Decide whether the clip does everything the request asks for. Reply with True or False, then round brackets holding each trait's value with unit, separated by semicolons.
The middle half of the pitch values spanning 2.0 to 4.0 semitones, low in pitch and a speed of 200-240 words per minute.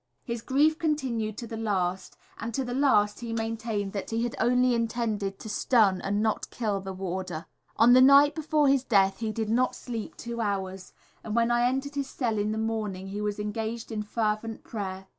False (2.9 semitones; 225 Hz; 205 wpm)